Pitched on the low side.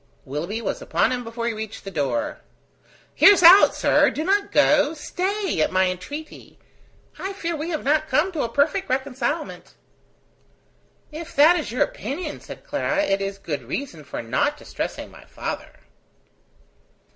No: very high, 290 Hz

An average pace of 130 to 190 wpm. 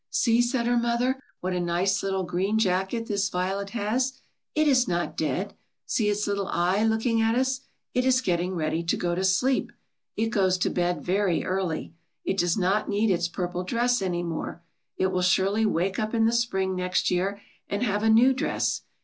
No: average, 200 wpm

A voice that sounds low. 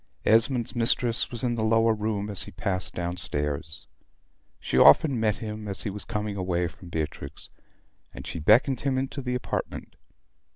Yes: low, 105 Hz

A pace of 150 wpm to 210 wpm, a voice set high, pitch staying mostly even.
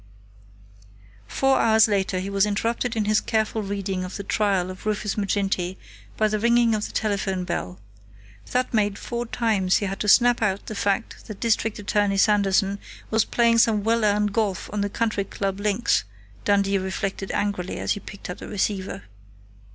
Yes: average, 180 wpm; high, 205 Hz; narrow, 2.1 semitones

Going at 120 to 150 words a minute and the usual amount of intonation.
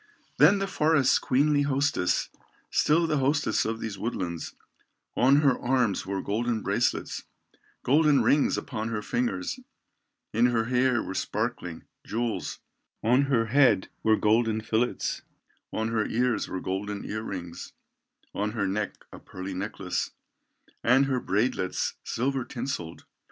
Yes: slow, 135 wpm; average, 4.3 semitones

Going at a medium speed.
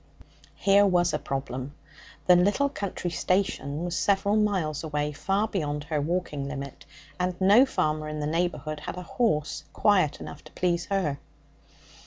Yes: average, 155 wpm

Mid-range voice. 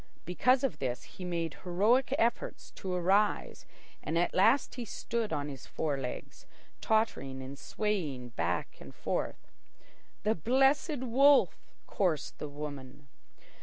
Yes: medium, 180 Hz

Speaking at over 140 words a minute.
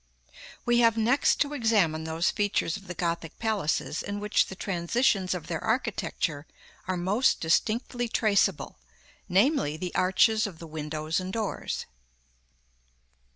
No: slow, 135 wpm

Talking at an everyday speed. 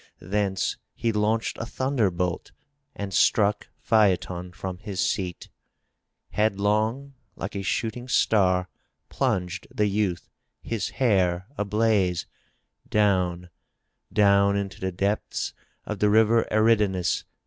No: slow, 110 wpm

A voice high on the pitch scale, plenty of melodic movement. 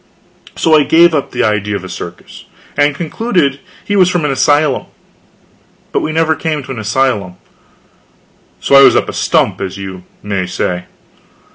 No: medium, 140 Hz; wide, 8.0 semitones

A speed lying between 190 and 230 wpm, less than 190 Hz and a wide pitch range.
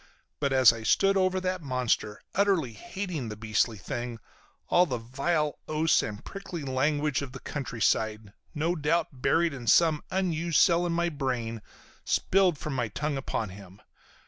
No: average, 160 wpm; medium, 140 Hz; wide, 6.5 semitones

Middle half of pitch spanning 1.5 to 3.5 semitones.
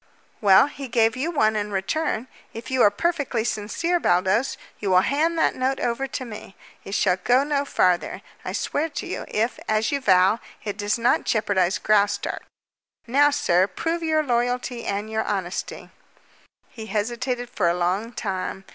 No: average, 5.0 semitones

